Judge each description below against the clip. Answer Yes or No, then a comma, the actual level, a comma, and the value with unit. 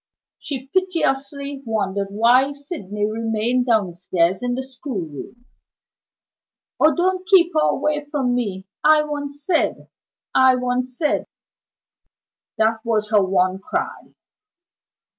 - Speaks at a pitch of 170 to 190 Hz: No, very high, 250 Hz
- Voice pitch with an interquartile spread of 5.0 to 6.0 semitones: Yes, wide, 5.4 semitones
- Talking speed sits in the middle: No, slow, 110 wpm